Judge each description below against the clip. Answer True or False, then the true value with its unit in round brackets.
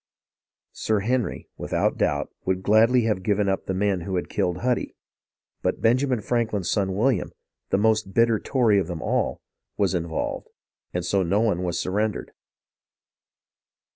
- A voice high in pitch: False (100 Hz)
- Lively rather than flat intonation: False (3.3 semitones)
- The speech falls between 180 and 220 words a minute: False (155 wpm)